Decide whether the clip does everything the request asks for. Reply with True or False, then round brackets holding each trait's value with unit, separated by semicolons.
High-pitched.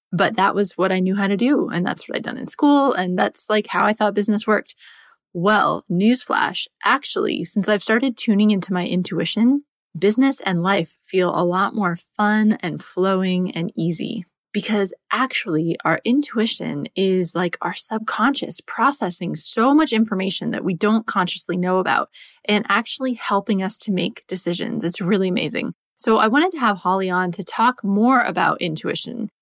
True (205 Hz)